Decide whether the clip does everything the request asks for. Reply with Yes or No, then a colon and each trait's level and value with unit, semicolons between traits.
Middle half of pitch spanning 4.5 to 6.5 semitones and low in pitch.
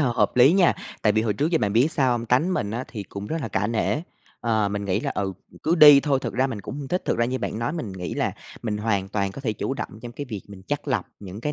Yes: average, 5.1 semitones; low, 115 Hz